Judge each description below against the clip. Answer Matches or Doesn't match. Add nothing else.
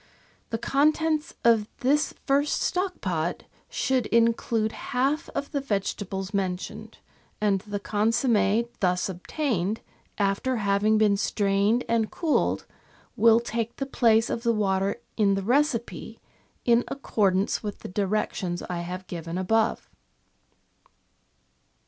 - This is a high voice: Matches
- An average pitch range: Matches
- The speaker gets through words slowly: Matches